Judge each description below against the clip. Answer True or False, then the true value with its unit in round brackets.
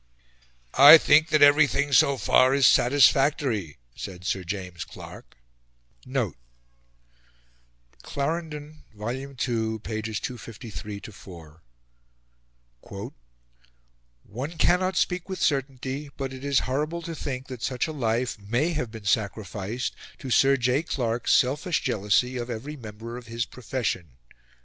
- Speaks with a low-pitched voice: True (125 Hz)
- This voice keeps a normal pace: False (115 wpm)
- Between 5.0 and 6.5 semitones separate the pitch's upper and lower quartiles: True (5.3 semitones)